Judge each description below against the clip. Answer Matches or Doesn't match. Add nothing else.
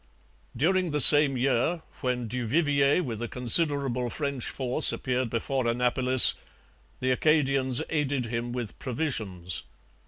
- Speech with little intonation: Doesn't match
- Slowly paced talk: Matches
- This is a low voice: Matches